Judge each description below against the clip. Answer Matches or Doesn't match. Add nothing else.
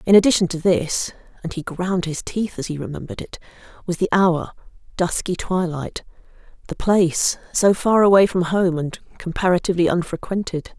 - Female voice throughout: Matches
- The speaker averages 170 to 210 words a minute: Doesn't match